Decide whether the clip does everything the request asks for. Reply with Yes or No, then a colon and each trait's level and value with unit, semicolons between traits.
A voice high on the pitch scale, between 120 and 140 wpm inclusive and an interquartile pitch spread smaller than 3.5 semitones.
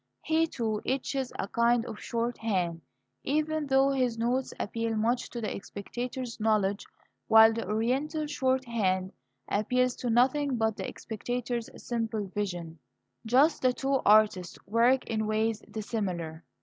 Yes: high, 230 Hz; slow, 135 wpm; average, 3.1 semitones